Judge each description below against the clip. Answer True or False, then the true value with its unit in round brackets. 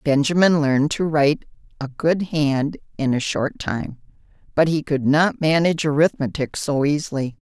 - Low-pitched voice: False (150 Hz)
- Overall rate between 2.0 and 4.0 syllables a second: False (4.9 syllables/s)